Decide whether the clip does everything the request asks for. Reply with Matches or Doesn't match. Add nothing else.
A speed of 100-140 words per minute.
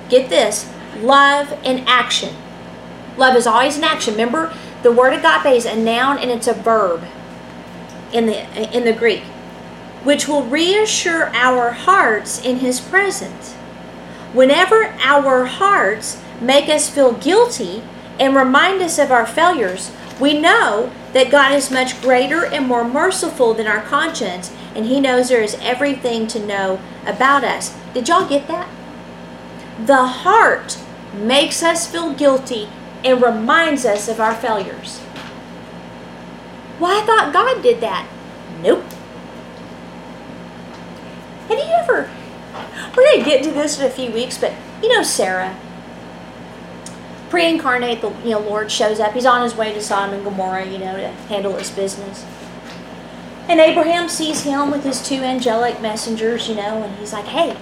Doesn't match